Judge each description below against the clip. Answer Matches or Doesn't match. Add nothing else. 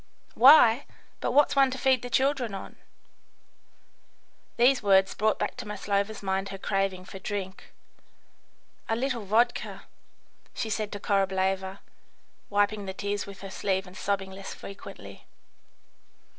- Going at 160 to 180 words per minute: Doesn't match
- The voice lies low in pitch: Doesn't match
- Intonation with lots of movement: Doesn't match